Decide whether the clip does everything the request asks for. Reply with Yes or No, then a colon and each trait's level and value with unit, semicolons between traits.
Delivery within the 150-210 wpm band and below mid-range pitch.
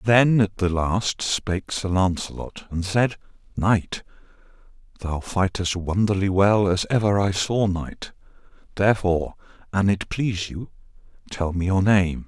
No: slow, 135 wpm; low, 100 Hz